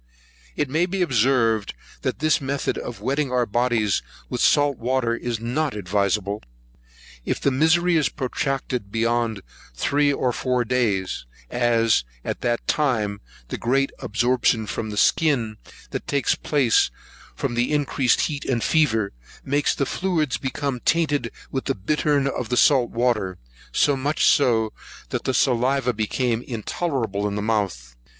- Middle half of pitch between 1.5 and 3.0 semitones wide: No, average, 4.0 semitones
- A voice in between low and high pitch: No, low, 125 Hz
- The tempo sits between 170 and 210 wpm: No, average, 145 wpm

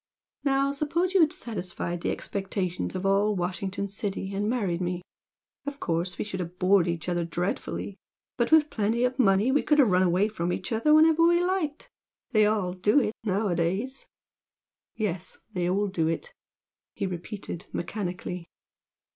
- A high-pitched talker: Yes, high, 200 Hz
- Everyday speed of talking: Yes, average, 165 wpm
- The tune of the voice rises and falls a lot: Yes, wide, 5.9 semitones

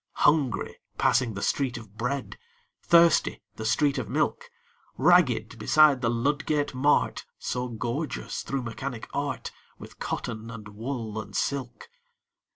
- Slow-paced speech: Yes, slow, 130 wpm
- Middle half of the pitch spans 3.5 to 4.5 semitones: Yes, average, 4.0 semitones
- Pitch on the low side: Yes, low, 125 Hz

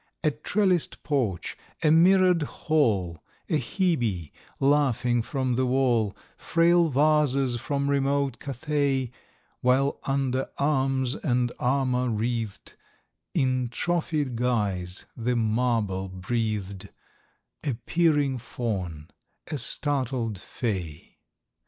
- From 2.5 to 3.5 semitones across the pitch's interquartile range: No, average, 4.1 semitones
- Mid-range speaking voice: No, low, 130 Hz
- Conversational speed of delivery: No, slow, 95 wpm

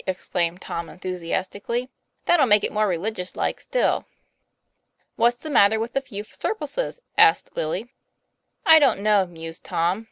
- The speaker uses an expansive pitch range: Yes, wide, 5.8 semitones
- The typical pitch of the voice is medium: No, high, 210 Hz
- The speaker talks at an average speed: Yes, average, 150 wpm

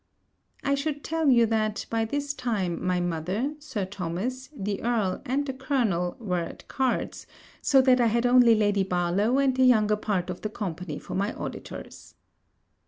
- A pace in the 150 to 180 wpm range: Yes, average, 170 wpm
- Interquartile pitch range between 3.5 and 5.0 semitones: No, wide, 5.5 semitones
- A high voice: Yes, high, 220 Hz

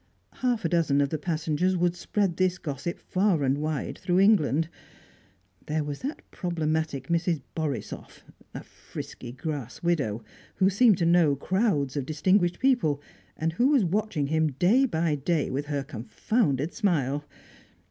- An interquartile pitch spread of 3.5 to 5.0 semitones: Yes, average, 4.5 semitones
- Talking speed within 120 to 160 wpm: Yes, average, 150 wpm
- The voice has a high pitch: No, medium, 160 Hz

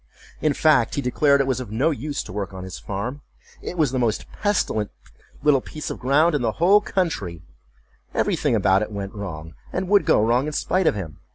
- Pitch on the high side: No, low, 130 Hz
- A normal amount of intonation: No, wide, 7.0 semitones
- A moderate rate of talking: No, fast, 215 wpm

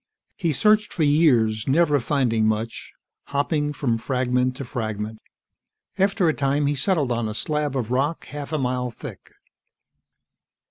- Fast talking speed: No, average, 145 wpm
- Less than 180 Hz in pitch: Yes, low, 135 Hz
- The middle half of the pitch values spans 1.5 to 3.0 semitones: No, average, 4.0 semitones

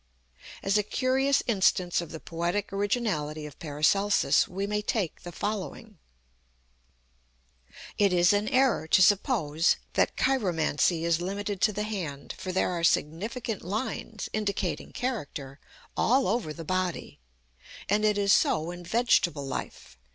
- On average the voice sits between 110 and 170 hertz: No, high, 195 Hz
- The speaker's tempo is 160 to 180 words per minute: No, slow, 135 wpm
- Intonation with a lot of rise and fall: No, average, 4.2 semitones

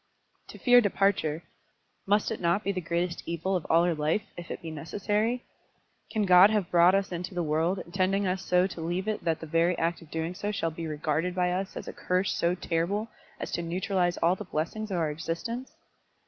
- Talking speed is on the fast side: Yes, fast, 215 wpm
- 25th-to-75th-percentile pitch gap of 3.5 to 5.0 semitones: No, average, 2.9 semitones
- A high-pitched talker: No, medium, 180 Hz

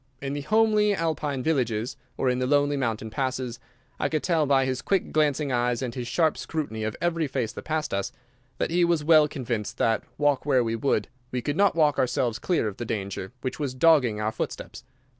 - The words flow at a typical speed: No, fast, 210 wpm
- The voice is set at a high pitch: No, low, 135 Hz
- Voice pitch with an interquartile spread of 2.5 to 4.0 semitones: No, average, 4.6 semitones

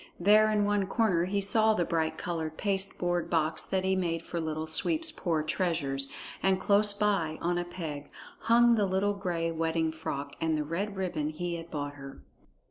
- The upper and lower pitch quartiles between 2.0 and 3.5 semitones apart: No, average, 3.9 semitones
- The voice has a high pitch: No, medium, 175 Hz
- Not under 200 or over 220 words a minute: No, average, 190 wpm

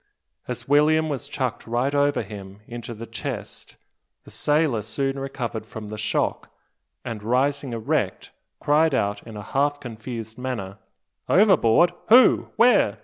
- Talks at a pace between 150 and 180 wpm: No, average, 140 wpm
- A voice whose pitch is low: Yes, low, 125 Hz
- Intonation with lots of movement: No, average, 4.6 semitones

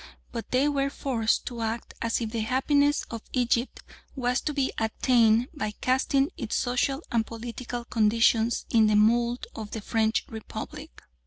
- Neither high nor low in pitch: No, high, 235 Hz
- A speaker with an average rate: Yes, average, 160 wpm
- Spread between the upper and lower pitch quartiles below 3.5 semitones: Yes, narrow, 2.6 semitones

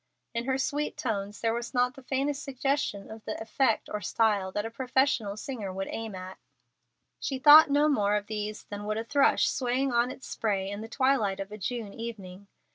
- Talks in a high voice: Yes, high, 225 Hz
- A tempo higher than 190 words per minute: Yes, average, 200 wpm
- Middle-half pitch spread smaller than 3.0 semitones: No, average, 4.3 semitones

